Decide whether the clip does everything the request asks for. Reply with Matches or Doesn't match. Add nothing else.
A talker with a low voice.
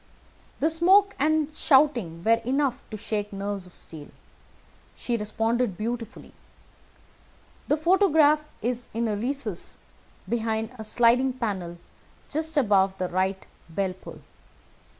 Doesn't match